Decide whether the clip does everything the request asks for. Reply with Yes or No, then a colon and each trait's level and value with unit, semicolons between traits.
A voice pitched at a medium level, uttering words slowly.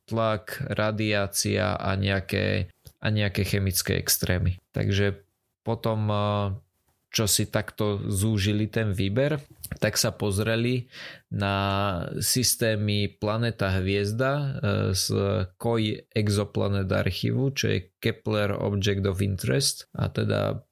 No: low, 105 Hz; slow, 100 wpm